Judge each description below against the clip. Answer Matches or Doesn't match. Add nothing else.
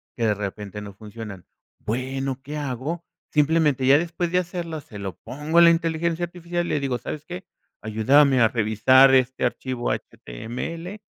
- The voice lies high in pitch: Doesn't match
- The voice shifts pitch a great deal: Matches